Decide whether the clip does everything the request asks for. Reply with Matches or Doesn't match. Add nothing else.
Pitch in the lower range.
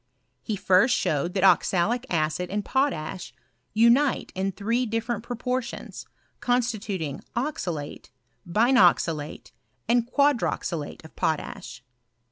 Doesn't match